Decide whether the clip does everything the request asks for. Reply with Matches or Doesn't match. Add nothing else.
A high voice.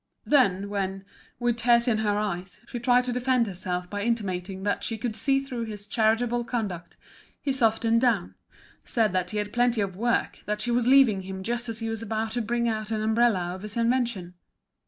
Matches